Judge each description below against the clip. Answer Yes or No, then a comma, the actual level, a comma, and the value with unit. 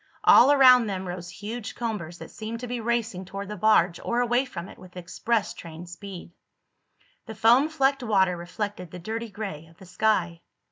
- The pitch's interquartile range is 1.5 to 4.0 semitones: No, average, 4.7 semitones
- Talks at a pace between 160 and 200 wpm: Yes, average, 185 wpm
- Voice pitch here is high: Yes, high, 205 Hz